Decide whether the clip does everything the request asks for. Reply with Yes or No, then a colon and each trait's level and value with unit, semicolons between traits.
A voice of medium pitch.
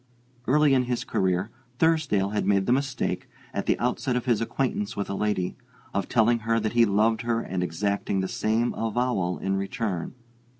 No: low, 110 Hz